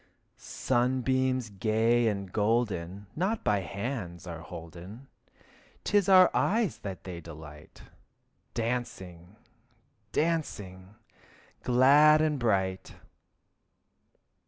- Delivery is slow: Yes, slow, 85 wpm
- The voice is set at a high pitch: No, low, 110 Hz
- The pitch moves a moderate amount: No, wide, 6.0 semitones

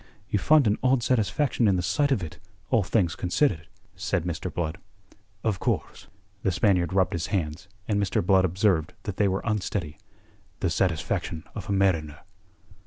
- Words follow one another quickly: No, average, 170 wpm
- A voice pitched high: No, very low, 95 Hz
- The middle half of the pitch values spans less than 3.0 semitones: No, average, 3.6 semitones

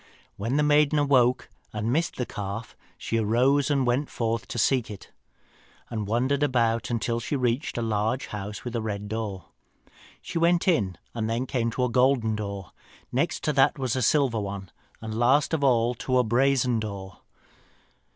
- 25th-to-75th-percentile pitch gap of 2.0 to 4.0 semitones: Yes, average, 3.4 semitones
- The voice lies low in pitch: Yes, low, 120 Hz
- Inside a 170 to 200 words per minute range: Yes, average, 180 wpm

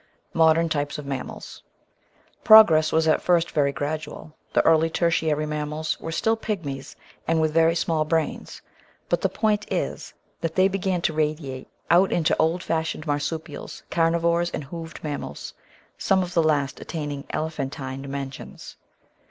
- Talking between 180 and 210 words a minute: No, average, 155 wpm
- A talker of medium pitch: Yes, medium, 160 Hz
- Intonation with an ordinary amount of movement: No, narrow, 2.3 semitones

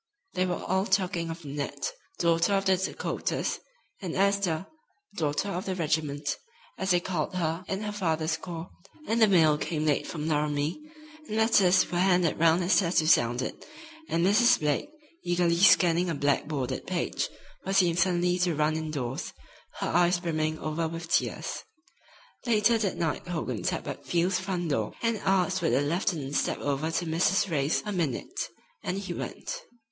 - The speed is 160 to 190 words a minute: Yes, average, 170 wpm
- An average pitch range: Yes, average, 3.3 semitones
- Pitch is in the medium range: Yes, medium, 170 Hz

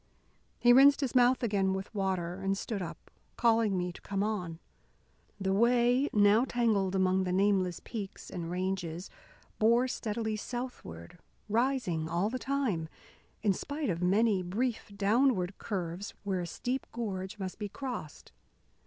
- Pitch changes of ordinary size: Yes, average, 4.4 semitones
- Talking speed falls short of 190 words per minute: Yes, average, 145 wpm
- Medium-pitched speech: No, high, 200 Hz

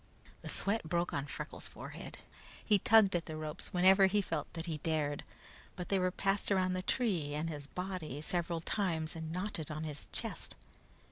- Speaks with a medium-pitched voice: Yes, medium, 175 Hz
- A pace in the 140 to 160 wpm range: No, average, 185 wpm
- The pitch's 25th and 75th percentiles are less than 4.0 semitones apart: Yes, average, 3.5 semitones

